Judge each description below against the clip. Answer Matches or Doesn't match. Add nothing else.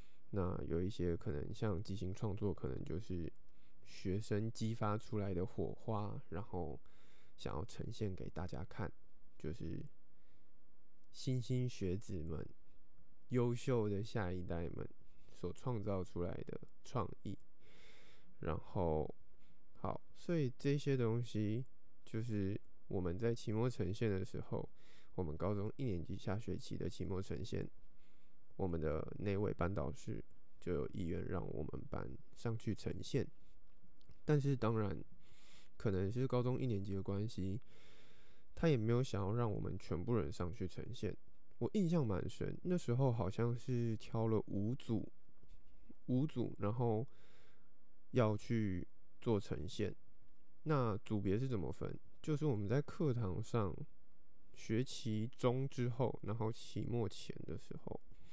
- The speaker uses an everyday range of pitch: Matches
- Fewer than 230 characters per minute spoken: Matches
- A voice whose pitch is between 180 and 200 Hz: Doesn't match